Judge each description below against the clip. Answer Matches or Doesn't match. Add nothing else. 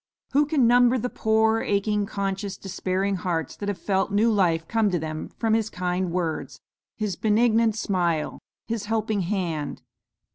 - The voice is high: Matches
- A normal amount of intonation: Matches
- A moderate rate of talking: Matches